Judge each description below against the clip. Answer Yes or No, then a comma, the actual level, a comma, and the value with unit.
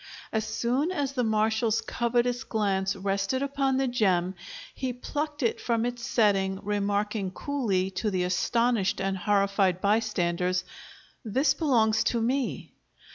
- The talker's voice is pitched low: No, high, 220 Hz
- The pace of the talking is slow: Yes, slow, 130 wpm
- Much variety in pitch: No, average, 4.1 semitones